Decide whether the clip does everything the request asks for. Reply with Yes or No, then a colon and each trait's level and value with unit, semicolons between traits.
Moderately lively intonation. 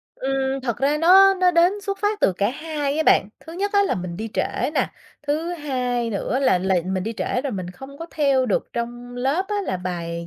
No: wide, 7.1 semitones